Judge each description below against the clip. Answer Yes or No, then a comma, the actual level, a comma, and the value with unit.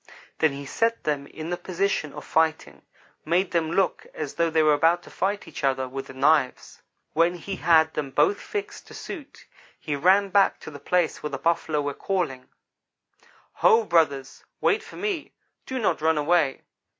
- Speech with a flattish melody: No, average, 4.6 semitones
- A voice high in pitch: No, medium, 160 Hz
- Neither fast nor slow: Yes, average, 185 wpm